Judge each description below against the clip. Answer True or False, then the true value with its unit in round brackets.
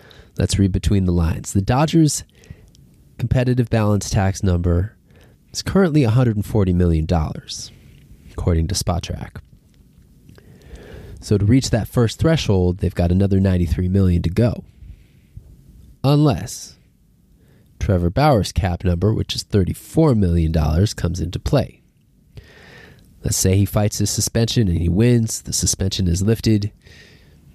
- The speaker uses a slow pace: True (120 wpm)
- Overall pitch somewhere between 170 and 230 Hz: False (100 Hz)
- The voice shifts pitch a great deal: False (4.6 semitones)